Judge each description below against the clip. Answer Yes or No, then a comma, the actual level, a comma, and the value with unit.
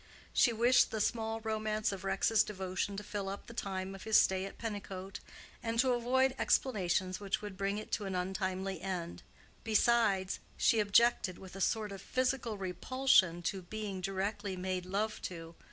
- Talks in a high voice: Yes, high, 200 Hz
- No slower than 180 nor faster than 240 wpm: No, average, 170 wpm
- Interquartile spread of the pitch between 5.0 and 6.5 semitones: No, average, 2.8 semitones